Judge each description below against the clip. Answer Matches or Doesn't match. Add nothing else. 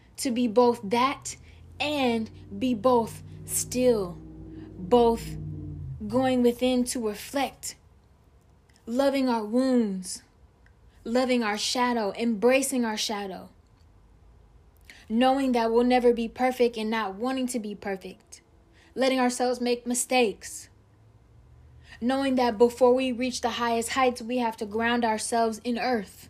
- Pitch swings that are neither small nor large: Matches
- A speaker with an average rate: Doesn't match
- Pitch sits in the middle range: Doesn't match